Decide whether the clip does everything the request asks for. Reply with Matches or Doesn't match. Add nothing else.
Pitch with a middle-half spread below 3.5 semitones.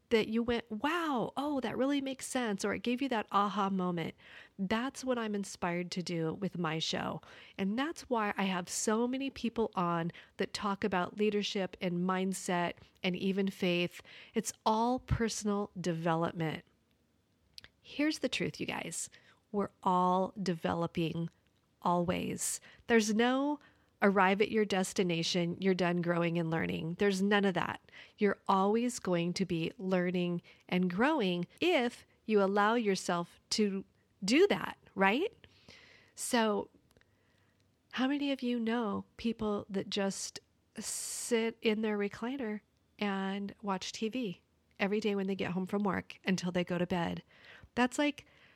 Doesn't match